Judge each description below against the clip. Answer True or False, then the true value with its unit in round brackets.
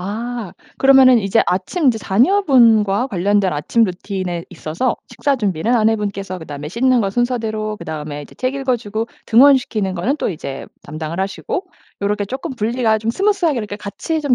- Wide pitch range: False (5.0 semitones)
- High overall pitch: True (215 Hz)